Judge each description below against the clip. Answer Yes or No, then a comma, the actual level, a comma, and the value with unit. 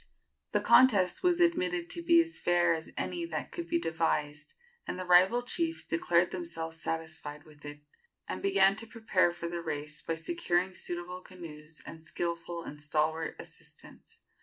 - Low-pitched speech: No, medium, 175 Hz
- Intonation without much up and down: No, wide, 5.4 semitones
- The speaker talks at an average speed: Yes, average, 160 wpm